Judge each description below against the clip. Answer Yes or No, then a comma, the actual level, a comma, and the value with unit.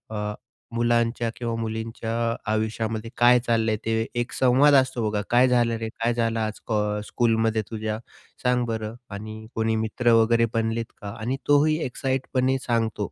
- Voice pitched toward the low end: Yes, low, 115 Hz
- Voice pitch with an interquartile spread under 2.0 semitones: Yes, narrow, 1.6 semitones